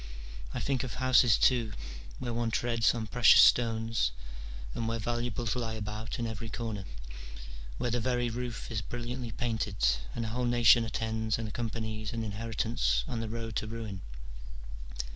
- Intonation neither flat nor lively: No, narrow, 1.5 semitones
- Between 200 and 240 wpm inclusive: No, average, 160 wpm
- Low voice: Yes, low, 115 Hz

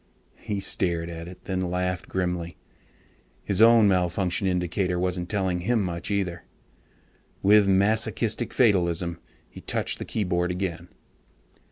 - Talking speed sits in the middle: No, slow, 125 wpm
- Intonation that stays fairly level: Yes, narrow, 2.3 semitones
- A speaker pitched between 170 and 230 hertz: No, very low, 90 Hz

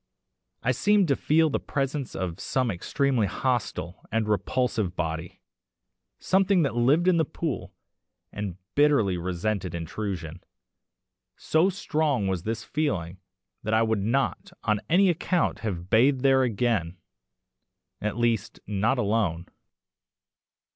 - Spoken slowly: Yes, slow, 125 wpm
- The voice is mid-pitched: No, low, 115 Hz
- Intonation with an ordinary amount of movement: No, wide, 6.9 semitones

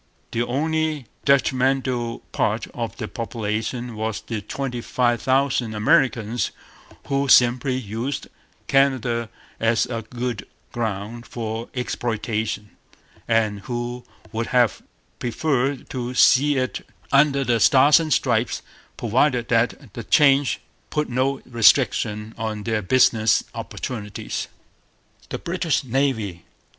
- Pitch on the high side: No, low, 120 Hz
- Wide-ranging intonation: No, average, 3.2 semitones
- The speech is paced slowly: Yes, slow, 110 wpm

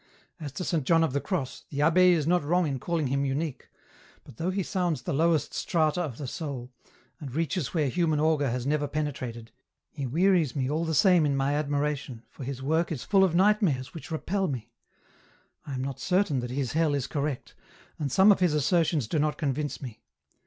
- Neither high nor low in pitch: Yes, medium, 150 Hz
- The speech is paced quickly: Yes, fast, 210 wpm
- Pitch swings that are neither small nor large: Yes, average, 3.8 semitones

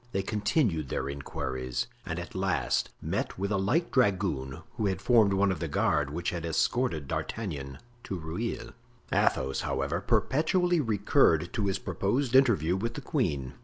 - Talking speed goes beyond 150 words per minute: Yes, average, 160 wpm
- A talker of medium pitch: No, very low, 95 Hz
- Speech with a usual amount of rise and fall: No, wide, 7.1 semitones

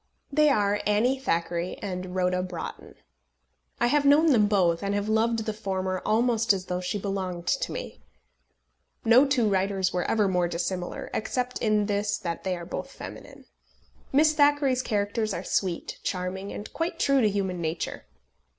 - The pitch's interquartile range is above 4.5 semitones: No, average, 4.2 semitones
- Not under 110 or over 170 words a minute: Yes, average, 165 wpm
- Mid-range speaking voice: No, high, 205 Hz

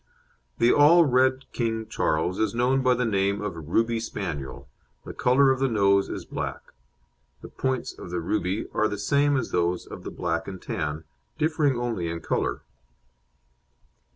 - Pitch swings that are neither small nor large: No, wide, 6.3 semitones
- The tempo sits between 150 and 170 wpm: Yes, average, 165 wpm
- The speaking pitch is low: Yes, low, 110 Hz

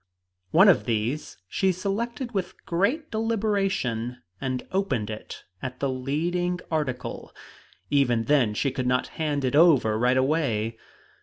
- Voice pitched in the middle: Yes, medium, 145 Hz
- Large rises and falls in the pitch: Yes, wide, 7.1 semitones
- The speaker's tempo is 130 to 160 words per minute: Yes, slow, 135 wpm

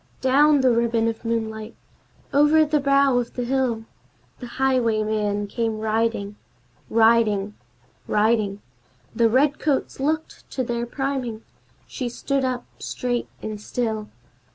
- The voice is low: No, high, 235 Hz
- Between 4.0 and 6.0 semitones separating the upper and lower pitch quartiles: No, average, 3.4 semitones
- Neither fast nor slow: No, slow, 120 wpm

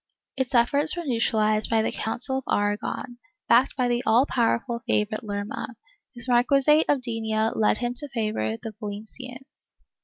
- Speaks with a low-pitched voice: No, high, 235 Hz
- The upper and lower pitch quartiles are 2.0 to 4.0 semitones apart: Yes, average, 3.0 semitones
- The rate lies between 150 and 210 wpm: Yes, average, 155 wpm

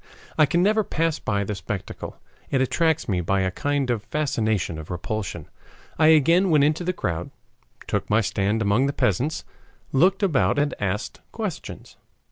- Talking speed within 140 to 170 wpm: Yes, average, 165 wpm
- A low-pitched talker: Yes, low, 130 Hz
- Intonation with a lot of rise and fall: Yes, wide, 7.7 semitones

